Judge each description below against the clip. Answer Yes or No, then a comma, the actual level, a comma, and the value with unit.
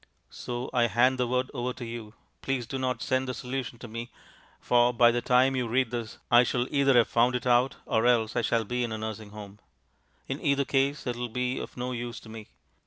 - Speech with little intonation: Yes, narrow, 1.5 semitones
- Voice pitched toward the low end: Yes, low, 120 Hz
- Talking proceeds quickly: Yes, fast, 235 wpm